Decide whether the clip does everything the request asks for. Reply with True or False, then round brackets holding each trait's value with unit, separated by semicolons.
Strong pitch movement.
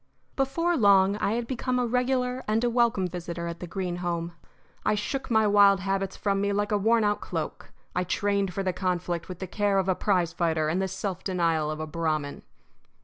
False (3.5 semitones)